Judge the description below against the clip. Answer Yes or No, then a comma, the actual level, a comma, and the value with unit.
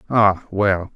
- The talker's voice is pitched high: No, low, 100 Hz